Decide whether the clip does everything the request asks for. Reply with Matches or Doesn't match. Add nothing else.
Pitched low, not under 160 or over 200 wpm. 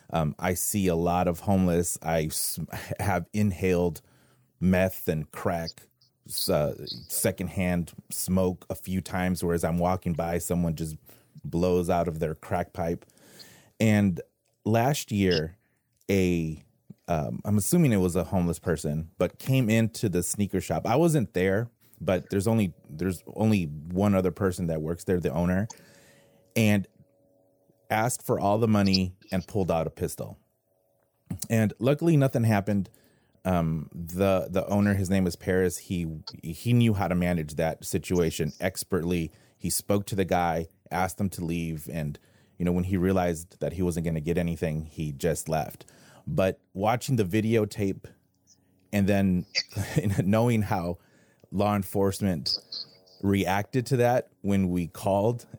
Doesn't match